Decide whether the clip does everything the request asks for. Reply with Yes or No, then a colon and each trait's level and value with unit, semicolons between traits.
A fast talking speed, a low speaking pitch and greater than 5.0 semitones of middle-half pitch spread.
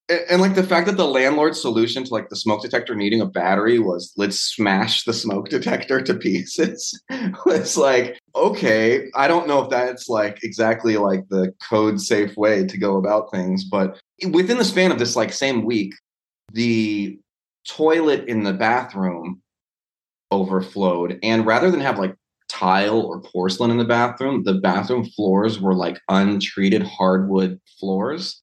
No: average, 165 wpm; low, 110 Hz; wide, 5.6 semitones